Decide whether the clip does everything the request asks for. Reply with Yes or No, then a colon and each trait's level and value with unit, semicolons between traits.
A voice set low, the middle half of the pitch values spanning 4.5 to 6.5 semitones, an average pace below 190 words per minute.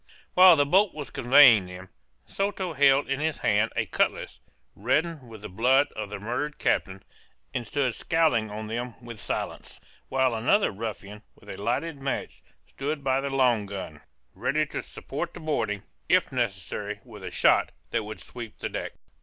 Yes: low, 120 Hz; average, 5.3 semitones; average, 170 wpm